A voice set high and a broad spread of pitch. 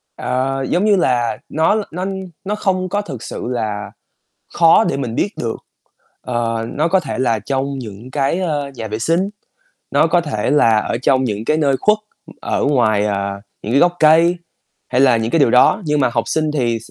No: low, 135 Hz; wide, 6.1 semitones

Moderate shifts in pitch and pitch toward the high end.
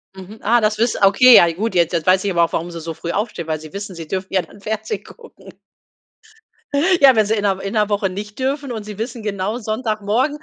Yes: average, 3.1 semitones; high, 205 Hz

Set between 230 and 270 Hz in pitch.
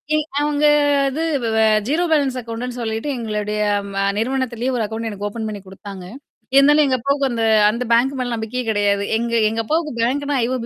Yes: high, 235 Hz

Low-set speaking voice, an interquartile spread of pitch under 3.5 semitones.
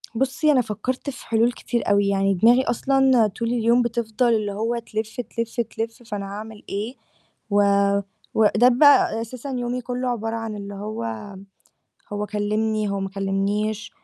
No: high, 225 Hz; average, 2.8 semitones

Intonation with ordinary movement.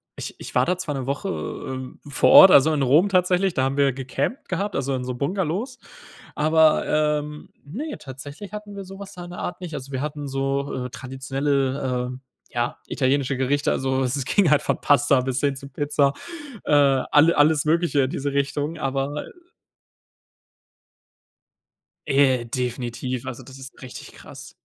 Yes: average, 3.2 semitones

